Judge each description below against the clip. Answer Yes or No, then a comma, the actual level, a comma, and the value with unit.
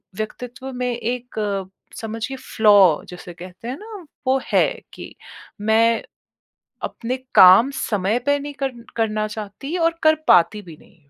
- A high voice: Yes, high, 225 Hz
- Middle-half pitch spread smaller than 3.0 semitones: No, average, 4.3 semitones